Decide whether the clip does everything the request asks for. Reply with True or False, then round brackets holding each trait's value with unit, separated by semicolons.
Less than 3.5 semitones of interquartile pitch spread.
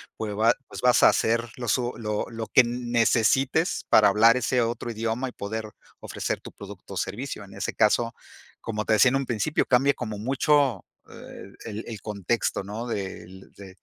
True (2.8 semitones)